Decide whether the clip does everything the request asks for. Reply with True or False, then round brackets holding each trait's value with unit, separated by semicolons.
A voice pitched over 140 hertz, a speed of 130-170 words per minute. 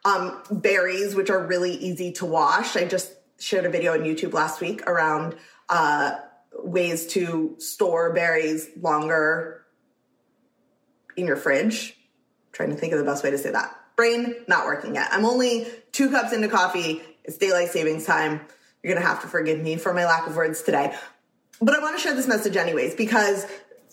False (190 Hz; 185 wpm)